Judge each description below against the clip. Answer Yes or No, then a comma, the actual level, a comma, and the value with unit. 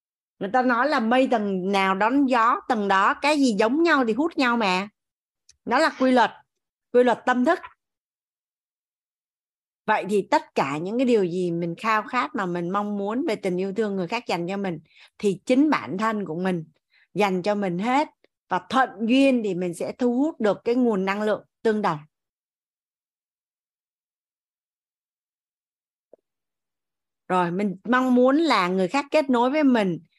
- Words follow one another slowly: No, average, 175 wpm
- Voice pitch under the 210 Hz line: No, high, 220 Hz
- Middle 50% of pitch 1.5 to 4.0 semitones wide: No, average, 5.1 semitones